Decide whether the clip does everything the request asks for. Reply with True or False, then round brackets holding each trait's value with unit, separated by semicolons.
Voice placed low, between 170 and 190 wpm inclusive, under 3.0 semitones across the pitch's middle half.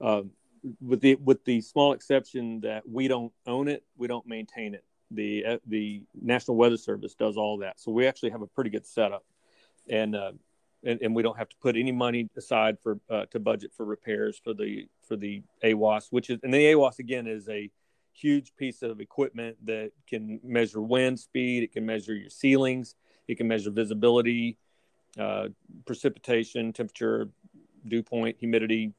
True (115 Hz; 180 wpm; 2.6 semitones)